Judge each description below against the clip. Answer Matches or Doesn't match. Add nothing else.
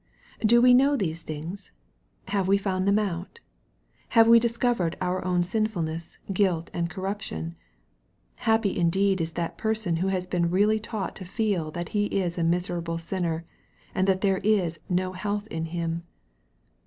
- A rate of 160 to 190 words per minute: Matches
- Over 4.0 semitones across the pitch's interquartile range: Doesn't match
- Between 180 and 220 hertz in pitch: Matches